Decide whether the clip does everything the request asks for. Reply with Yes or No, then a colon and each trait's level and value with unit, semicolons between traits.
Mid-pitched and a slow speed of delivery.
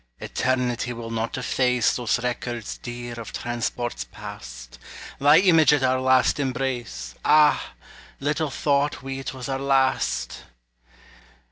No: low, 125 Hz; slow, 125 wpm